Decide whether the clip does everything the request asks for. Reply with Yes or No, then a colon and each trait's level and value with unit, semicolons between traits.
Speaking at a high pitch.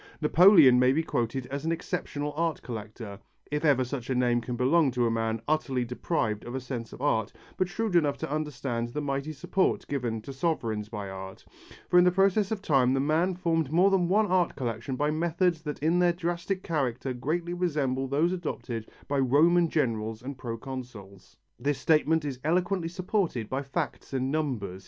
No: medium, 140 Hz